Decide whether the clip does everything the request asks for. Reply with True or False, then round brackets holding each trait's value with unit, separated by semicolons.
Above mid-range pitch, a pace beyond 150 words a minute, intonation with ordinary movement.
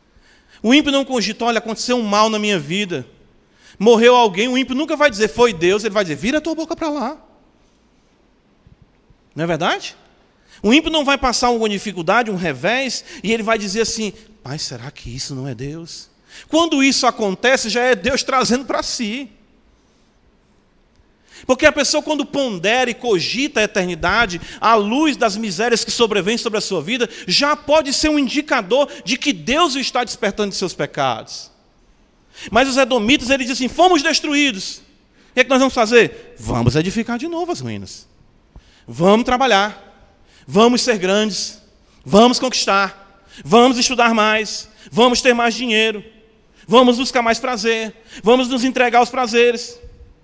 True (235 Hz; 165 wpm; 4.1 semitones)